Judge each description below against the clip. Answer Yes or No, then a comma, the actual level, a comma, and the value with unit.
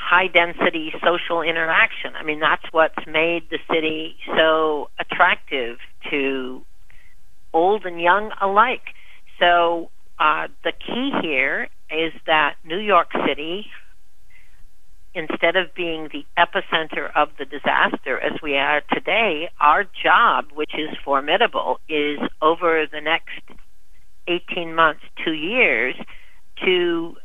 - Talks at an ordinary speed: No, slow, 120 wpm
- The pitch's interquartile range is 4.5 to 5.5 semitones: No, narrow, 2.4 semitones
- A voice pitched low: No, medium, 165 Hz